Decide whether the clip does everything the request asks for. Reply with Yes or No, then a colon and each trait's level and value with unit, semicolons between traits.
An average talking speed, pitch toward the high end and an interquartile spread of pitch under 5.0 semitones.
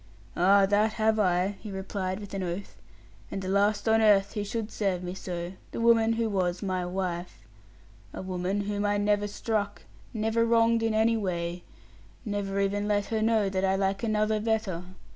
Yes: average, 180 wpm; high, 205 Hz; narrow, 2.5 semitones